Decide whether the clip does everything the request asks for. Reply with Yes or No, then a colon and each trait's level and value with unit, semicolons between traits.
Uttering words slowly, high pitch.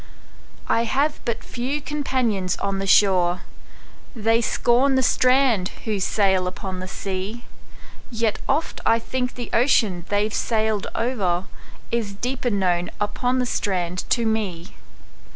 Yes: slow, 120 wpm; high, 220 Hz